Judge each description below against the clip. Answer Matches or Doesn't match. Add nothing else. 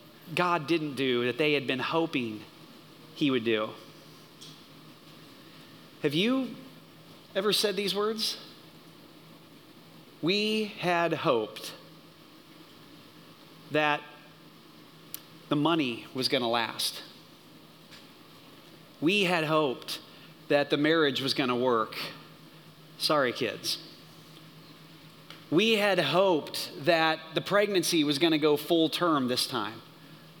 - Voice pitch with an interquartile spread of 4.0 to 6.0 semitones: Doesn't match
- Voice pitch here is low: Doesn't match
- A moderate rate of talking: Doesn't match